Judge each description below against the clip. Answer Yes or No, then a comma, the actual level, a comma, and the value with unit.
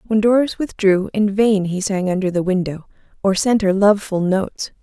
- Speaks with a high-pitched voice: Yes, high, 200 Hz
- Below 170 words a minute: No, average, 200 wpm